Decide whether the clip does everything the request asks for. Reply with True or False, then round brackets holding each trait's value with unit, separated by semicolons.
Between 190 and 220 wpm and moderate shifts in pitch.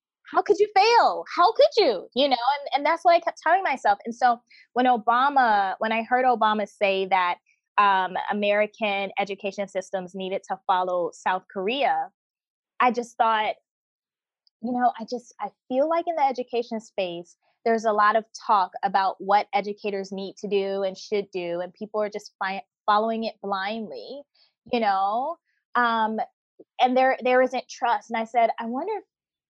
False (175 wpm; 4.8 semitones)